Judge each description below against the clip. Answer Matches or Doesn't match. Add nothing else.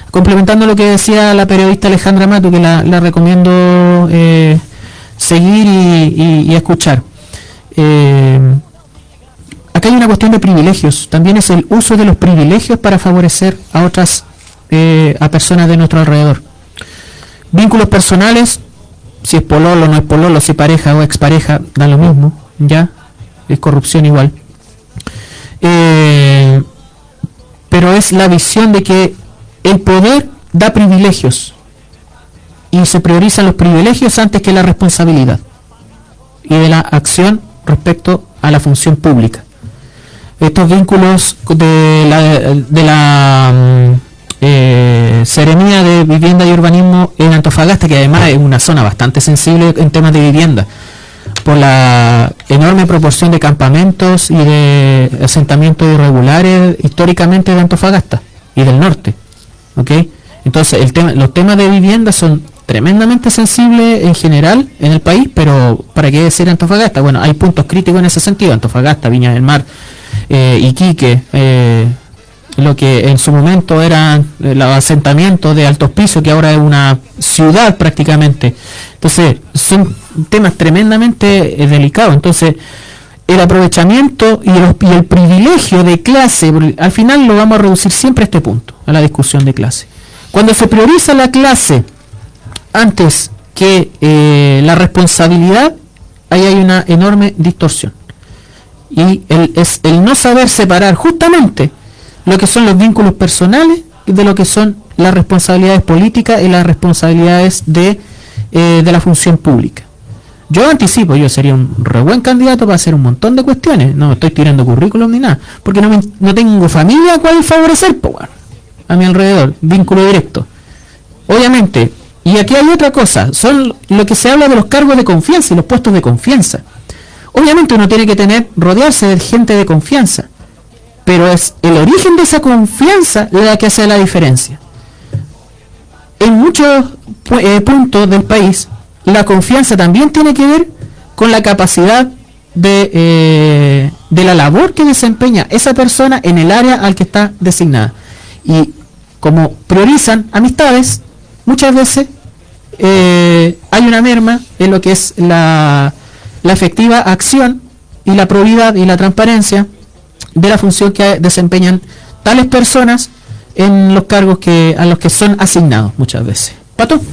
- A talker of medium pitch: Matches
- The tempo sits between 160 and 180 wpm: Doesn't match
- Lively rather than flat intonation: Matches